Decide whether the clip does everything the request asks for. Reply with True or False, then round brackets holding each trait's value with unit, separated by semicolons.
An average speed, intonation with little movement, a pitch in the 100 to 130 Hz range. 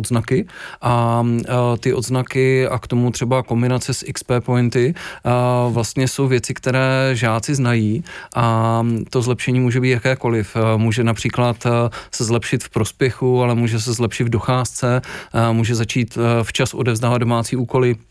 True (145 wpm; 1.5 semitones; 120 Hz)